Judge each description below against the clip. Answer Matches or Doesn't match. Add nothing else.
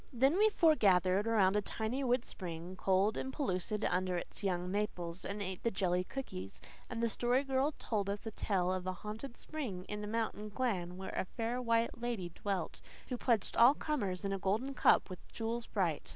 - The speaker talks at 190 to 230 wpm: Matches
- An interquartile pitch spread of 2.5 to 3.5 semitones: Doesn't match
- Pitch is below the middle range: Doesn't match